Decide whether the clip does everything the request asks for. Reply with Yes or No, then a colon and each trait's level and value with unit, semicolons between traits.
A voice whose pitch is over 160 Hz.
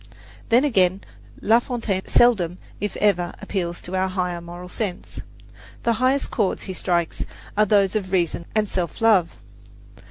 Yes: high, 190 Hz